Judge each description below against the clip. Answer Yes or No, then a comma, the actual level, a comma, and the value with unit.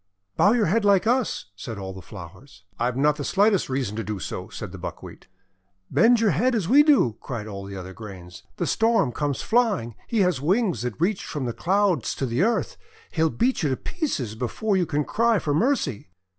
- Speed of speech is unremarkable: No, fast, 210 wpm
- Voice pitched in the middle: Yes, medium, 150 Hz